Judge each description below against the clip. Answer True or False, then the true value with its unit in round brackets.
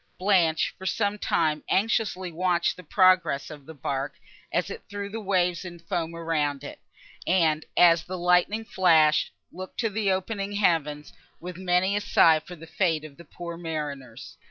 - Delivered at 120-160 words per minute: False (170 wpm)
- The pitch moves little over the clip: False (3.0 semitones)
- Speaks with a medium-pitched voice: True (175 Hz)